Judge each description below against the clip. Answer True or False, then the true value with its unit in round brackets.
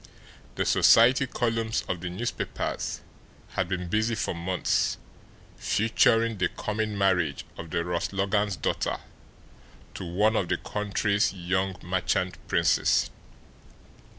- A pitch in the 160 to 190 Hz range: False (100 Hz)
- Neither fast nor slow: False (120 wpm)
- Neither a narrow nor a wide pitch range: True (3.4 semitones)